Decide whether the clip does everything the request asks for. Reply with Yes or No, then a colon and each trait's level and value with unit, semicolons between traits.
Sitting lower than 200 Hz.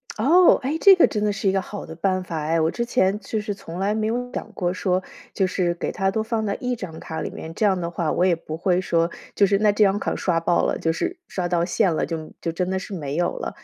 Yes: high, 190 Hz